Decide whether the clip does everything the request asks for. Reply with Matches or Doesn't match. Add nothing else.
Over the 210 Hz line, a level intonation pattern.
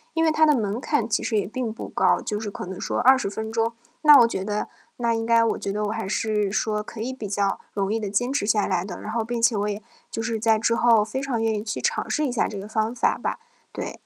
Matches